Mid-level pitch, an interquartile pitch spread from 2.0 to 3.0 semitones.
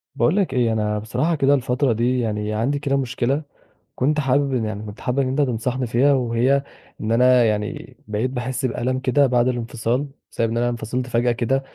No: low, 125 Hz; average, 2.7 semitones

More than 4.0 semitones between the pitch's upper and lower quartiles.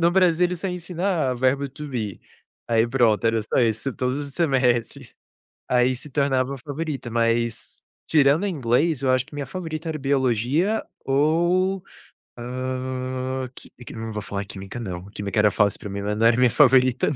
Yes: average, 4.4 semitones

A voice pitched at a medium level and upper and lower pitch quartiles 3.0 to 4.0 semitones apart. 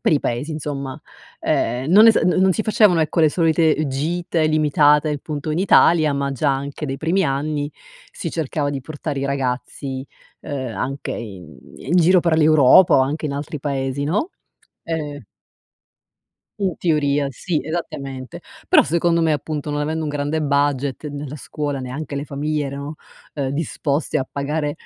No: medium, 145 Hz; narrow, 2.4 semitones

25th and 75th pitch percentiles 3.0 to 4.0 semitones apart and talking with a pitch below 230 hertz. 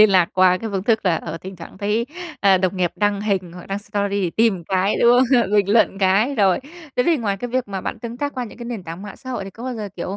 Yes: average, 3.7 semitones; high, 200 Hz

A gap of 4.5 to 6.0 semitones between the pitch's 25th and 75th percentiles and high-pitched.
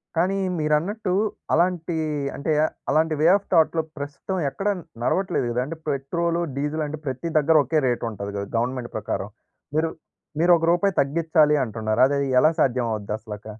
No: average, 5.0 semitones; medium, 150 Hz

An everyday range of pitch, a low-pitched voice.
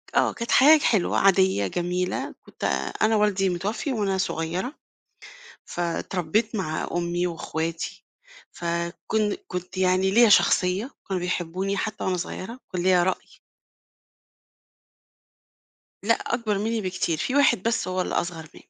No: average, 3.5 semitones; medium, 185 Hz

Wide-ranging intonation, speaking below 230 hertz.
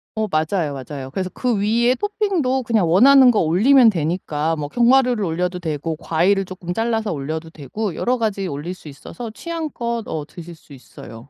Yes: wide, 6.8 semitones; medium, 185 Hz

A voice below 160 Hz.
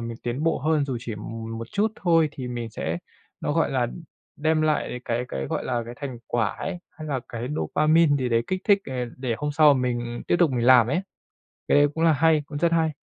Yes: low, 135 Hz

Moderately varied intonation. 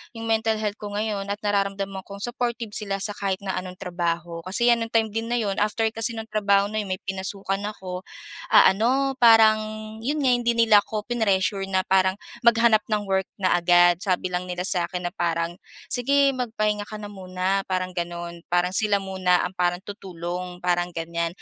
Yes: average, 3.3 semitones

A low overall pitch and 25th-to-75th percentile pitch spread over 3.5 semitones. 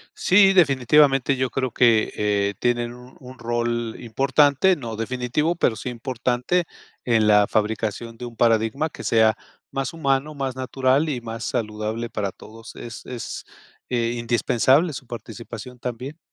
No: low, 120 Hz; average, 2.9 semitones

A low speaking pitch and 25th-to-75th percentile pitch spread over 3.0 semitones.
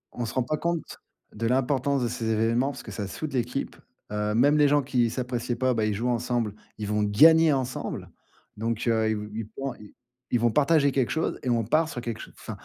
Yes: low, 120 Hz; average, 3.6 semitones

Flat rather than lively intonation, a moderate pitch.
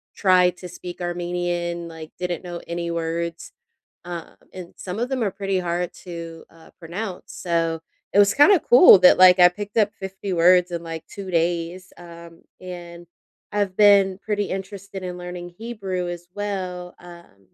Yes: narrow, 2.1 semitones; medium, 180 Hz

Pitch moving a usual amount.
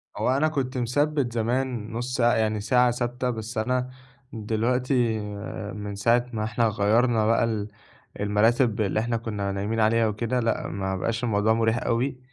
No: narrow, 2.3 semitones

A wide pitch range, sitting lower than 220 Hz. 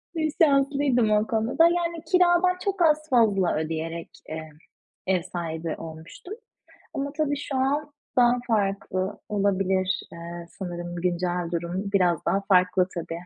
Yes: wide, 8.4 semitones; high, 195 Hz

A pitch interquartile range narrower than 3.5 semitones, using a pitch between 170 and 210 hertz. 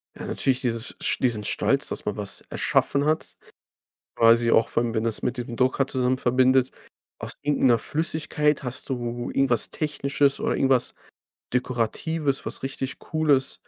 No: average, 2.7 semitones; low, 130 Hz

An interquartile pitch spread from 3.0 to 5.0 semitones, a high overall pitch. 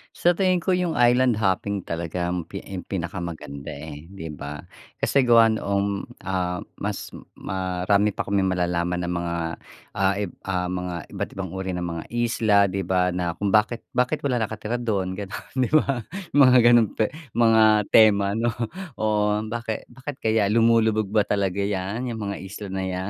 No: average, 3.8 semitones; low, 100 Hz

